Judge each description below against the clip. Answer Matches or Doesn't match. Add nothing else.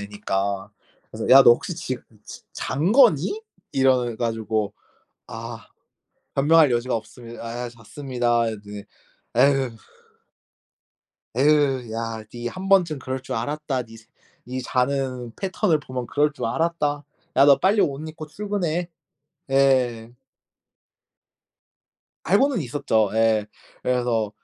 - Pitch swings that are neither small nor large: Matches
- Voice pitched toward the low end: Matches